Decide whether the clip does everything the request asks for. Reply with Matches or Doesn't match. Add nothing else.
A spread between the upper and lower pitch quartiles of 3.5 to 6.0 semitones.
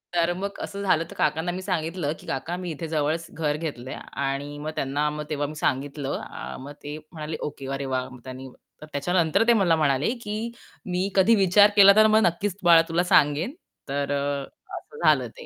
Matches